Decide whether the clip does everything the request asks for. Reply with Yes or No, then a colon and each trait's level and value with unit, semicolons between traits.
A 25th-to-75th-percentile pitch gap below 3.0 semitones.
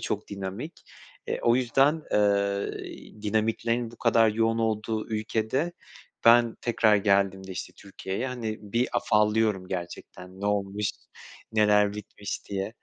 Yes: narrow, 2.4 semitones